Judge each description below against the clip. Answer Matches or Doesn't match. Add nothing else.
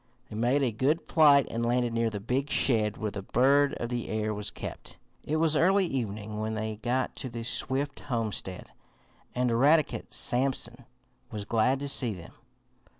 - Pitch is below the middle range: Matches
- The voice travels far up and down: Doesn't match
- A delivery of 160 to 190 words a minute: Matches